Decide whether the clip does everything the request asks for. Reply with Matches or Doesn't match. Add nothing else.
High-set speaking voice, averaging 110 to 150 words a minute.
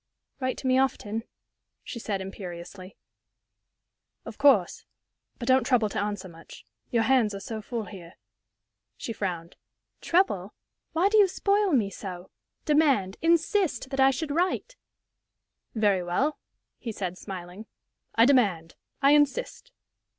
Matches